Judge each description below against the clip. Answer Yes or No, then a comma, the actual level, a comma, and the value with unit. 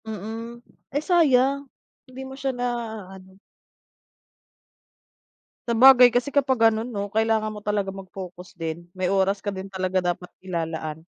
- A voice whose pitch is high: Yes, high, 210 Hz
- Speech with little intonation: No, average, 4.8 semitones